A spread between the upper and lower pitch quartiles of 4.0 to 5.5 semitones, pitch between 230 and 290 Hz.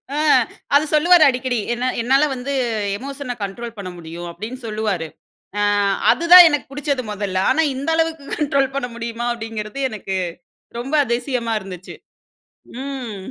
Yes: average, 4.3 semitones; very high, 250 Hz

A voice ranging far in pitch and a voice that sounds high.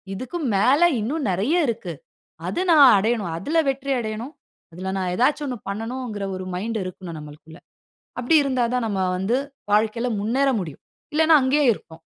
Yes: wide, 5.7 semitones; high, 225 Hz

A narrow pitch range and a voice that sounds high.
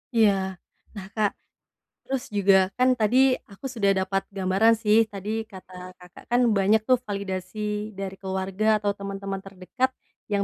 Yes: narrow, 2.1 semitones; high, 200 Hz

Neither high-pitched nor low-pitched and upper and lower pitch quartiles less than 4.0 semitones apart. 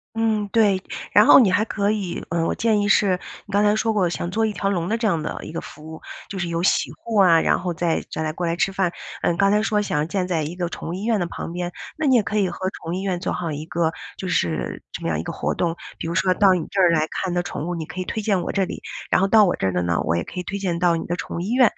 Yes: medium, 180 Hz; average, 3.4 semitones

